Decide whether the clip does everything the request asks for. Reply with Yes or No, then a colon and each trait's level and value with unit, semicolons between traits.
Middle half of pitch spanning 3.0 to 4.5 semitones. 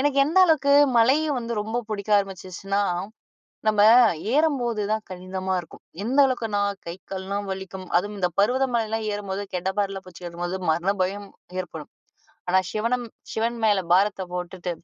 Yes: average, 3.6 semitones